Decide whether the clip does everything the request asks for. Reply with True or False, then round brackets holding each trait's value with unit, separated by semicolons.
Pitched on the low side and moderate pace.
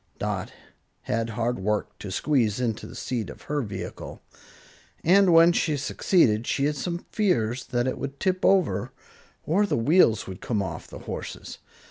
True (130 Hz; 165 wpm)